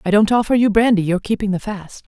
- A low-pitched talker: No, high, 205 Hz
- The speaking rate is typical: No, fast, 250 wpm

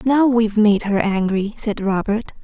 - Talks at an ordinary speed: Yes, average, 170 wpm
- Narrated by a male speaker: No, female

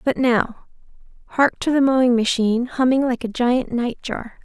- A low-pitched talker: No, high, 245 Hz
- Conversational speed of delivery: Yes, average, 160 wpm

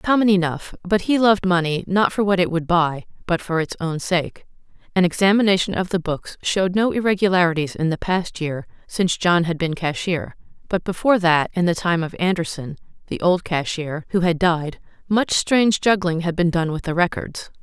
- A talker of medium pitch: Yes, medium, 175 Hz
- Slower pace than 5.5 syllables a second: Yes, 5.3 syllables/s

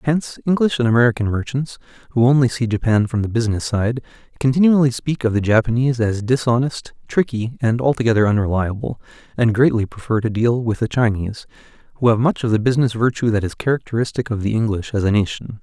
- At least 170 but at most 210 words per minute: Yes, average, 185 wpm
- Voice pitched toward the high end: No, low, 120 Hz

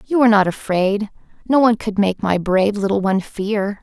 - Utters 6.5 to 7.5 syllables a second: No, 5.6 syllables/s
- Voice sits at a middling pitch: No, high, 205 Hz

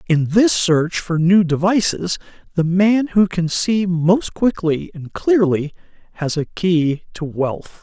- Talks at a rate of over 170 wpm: No, average, 155 wpm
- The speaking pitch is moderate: Yes, medium, 175 Hz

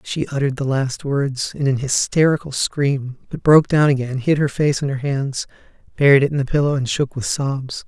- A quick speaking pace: Yes, fast, 215 wpm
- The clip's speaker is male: Yes, male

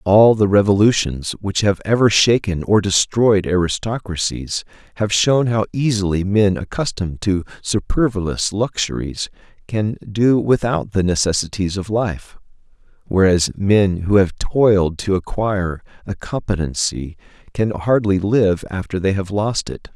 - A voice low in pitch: Yes, low, 100 Hz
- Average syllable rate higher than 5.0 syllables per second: No, 4.3 syllables/s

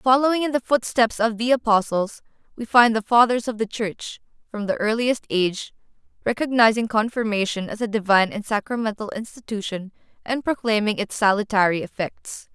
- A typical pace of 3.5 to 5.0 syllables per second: No, 5.4 syllables/s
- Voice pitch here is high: Yes, high, 220 Hz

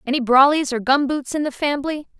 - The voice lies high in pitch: Yes, very high, 275 Hz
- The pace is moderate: Yes, average, 190 wpm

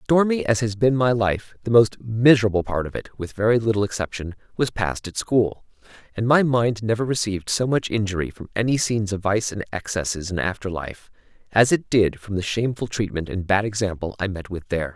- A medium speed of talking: No, fast, 210 wpm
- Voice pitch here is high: No, low, 105 Hz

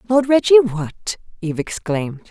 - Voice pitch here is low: No, high, 205 Hz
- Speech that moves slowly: Yes, slow, 130 wpm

